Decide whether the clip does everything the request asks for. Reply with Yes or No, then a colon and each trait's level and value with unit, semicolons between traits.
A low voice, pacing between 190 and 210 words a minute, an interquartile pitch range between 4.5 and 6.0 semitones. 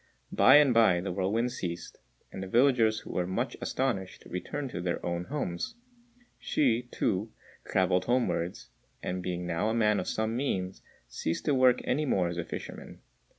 No: low, 100 Hz; average, 170 wpm; wide, 5.6 semitones